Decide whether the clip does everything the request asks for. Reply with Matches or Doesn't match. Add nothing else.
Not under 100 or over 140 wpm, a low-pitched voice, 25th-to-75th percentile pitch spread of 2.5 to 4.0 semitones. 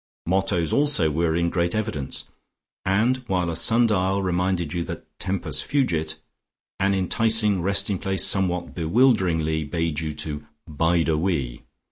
Matches